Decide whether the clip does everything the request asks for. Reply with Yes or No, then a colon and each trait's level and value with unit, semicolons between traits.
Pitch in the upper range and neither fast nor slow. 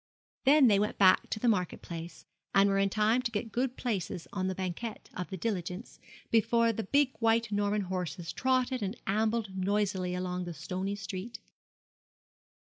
Yes: high, 205 Hz; average, 170 wpm